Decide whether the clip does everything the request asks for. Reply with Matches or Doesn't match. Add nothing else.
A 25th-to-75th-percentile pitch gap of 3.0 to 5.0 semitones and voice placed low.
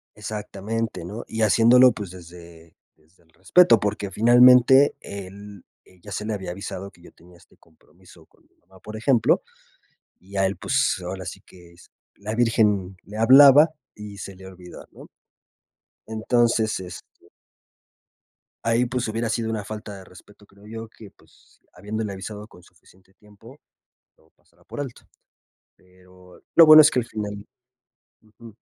Matches